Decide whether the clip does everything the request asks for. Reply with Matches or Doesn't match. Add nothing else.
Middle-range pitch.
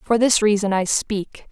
Doesn't match